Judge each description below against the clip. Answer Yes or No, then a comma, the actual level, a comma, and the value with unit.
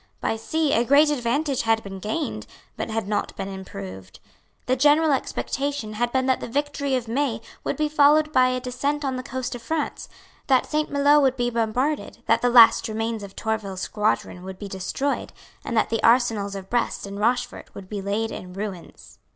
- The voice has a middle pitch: No, high, 240 Hz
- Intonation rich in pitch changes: No, average, 4.9 semitones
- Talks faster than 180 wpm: Yes, average, 195 wpm